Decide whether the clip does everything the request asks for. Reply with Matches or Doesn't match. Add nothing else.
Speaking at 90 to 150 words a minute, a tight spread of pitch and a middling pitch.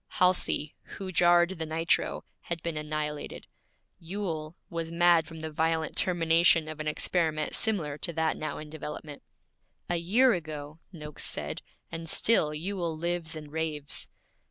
Matches